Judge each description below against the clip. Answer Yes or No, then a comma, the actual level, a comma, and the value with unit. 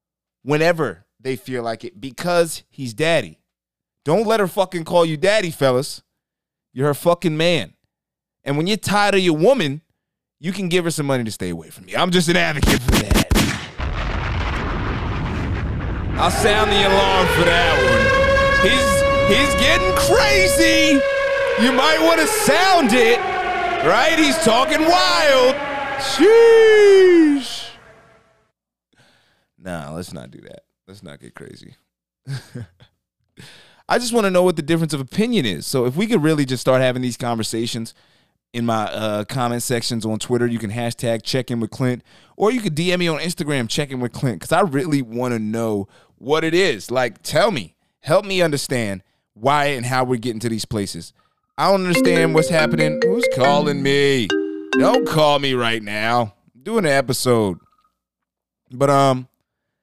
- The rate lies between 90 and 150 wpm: No, average, 165 wpm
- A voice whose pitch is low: No, medium, 145 Hz